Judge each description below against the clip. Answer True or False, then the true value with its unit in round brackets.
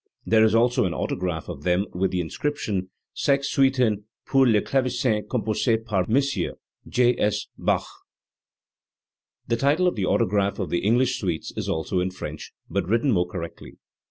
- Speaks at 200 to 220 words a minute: False (165 wpm)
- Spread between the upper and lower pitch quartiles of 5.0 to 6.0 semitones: True (5.4 semitones)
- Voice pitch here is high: False (110 Hz)